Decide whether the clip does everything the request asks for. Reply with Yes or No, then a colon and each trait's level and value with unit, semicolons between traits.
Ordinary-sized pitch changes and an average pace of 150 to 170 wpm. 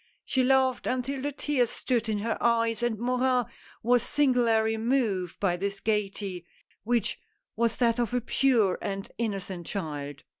Yes: average, 3.8 semitones; average, 155 wpm